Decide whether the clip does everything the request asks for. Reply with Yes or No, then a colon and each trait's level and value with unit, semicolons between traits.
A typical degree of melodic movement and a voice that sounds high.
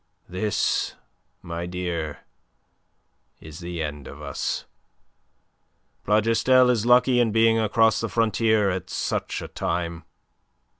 No: average, 5.0 semitones; low, 100 Hz